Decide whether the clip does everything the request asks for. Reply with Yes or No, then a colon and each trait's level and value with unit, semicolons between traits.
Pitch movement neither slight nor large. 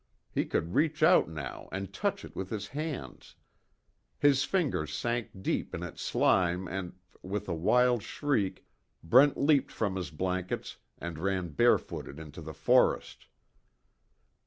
No: wide, 7.2 semitones